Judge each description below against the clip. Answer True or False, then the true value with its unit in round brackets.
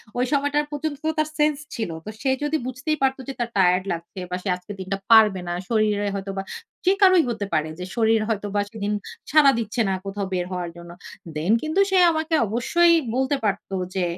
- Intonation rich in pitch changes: True (7.1 semitones)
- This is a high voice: True (220 Hz)